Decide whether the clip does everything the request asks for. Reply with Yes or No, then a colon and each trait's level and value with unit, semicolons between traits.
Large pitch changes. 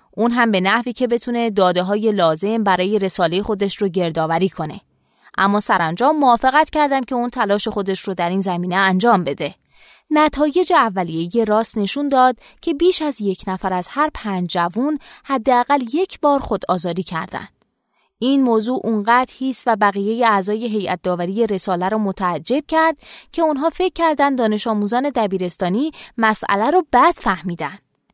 Yes: wide, 5.7 semitones